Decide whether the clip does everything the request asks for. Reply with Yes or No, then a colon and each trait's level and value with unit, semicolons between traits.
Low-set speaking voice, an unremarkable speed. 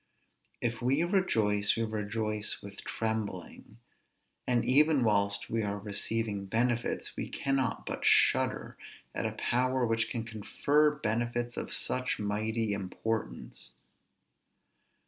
No: low, 115 Hz; slow, 115 wpm